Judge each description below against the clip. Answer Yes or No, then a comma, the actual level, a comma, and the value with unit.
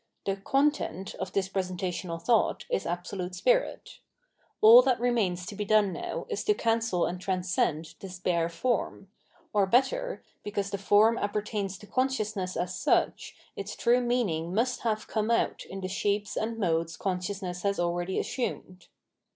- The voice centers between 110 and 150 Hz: No, high, 200 Hz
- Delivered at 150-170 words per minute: Yes, average, 160 wpm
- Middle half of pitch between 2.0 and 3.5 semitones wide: No, average, 4.0 semitones